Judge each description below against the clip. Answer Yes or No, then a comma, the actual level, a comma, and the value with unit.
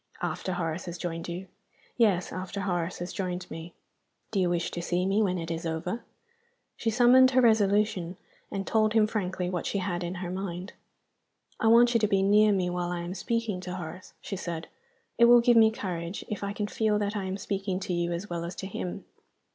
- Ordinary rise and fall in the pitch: Yes, average, 3.2 semitones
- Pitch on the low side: No, medium, 185 Hz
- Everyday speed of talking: No, fast, 215 wpm